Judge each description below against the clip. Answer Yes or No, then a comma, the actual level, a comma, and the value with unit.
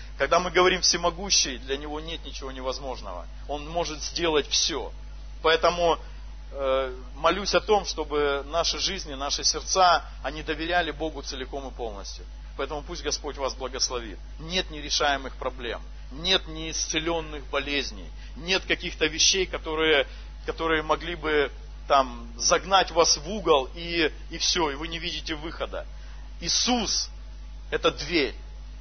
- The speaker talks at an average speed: Yes, average, 130 wpm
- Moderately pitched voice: Yes, medium, 155 Hz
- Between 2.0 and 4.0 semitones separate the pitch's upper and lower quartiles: Yes, average, 3.7 semitones